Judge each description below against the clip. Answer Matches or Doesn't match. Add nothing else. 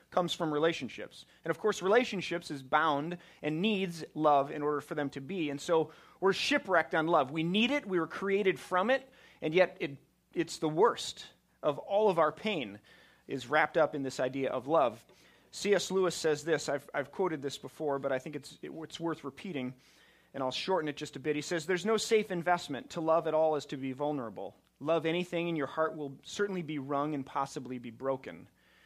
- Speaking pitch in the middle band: Matches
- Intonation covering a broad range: Doesn't match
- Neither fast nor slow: Doesn't match